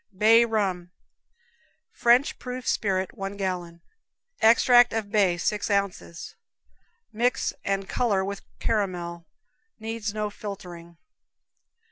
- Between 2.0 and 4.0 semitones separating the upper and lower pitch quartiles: Yes, average, 3.4 semitones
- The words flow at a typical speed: No, slow, 95 wpm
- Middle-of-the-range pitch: No, high, 200 Hz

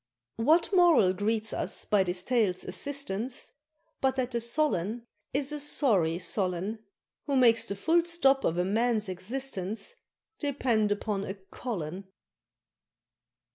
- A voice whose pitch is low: No, high, 225 Hz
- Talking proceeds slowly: Yes, slow, 130 wpm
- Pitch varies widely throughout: Yes, wide, 5.8 semitones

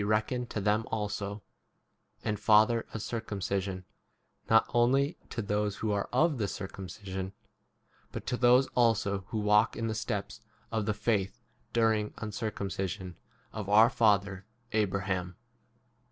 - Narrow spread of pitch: Yes, narrow, 2.2 semitones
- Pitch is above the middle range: No, low, 105 Hz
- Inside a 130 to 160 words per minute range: Yes, average, 140 wpm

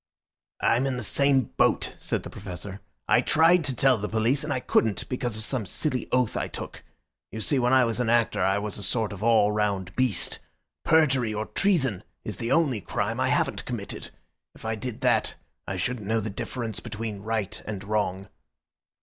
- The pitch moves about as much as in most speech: Yes, average, 3.6 semitones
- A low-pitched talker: Yes, low, 115 Hz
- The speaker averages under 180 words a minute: No, average, 195 wpm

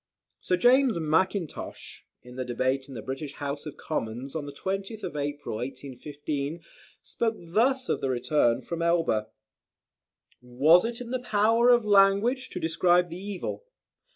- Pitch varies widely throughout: Yes, wide, 6.8 semitones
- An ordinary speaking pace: Yes, average, 150 wpm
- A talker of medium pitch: Yes, medium, 165 Hz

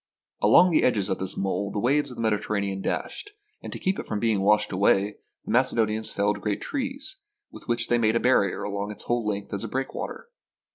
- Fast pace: Yes, fast, 210 wpm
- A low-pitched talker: Yes, low, 110 Hz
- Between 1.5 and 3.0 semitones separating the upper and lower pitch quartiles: No, average, 3.5 semitones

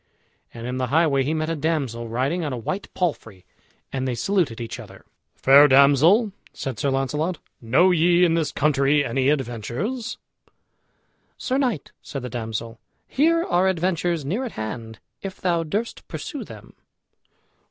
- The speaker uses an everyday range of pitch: No, wide, 5.9 semitones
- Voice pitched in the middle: Yes, medium, 150 Hz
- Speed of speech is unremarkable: Yes, average, 155 wpm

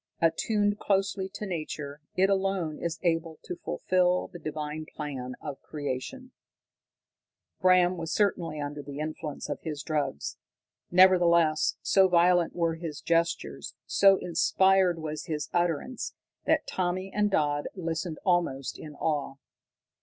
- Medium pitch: Yes, medium, 170 Hz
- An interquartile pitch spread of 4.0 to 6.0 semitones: No, average, 3.3 semitones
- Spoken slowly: Yes, slow, 130 wpm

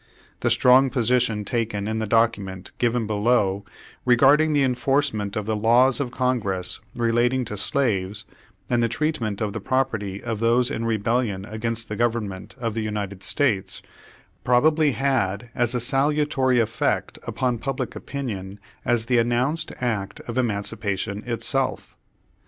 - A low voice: Yes, low, 115 Hz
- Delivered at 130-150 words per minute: Yes, average, 140 wpm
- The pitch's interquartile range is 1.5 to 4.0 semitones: Yes, average, 3.5 semitones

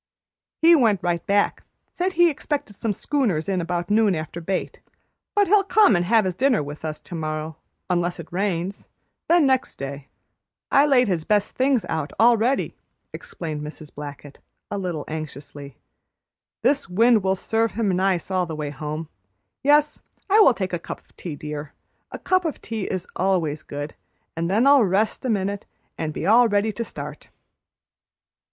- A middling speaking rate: Yes, average, 175 wpm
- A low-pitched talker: No, high, 190 Hz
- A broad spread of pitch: Yes, wide, 6.7 semitones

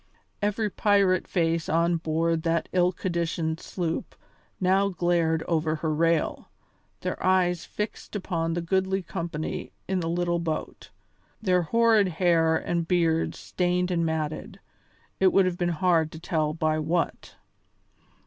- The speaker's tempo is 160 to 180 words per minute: No, average, 140 wpm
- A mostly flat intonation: Yes, narrow, 2.1 semitones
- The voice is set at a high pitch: No, medium, 170 Hz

